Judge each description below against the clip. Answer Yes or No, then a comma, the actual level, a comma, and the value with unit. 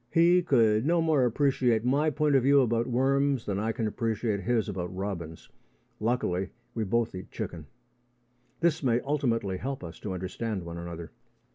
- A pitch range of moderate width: No, wide, 6.0 semitones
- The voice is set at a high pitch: No, low, 115 Hz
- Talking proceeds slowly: No, average, 165 wpm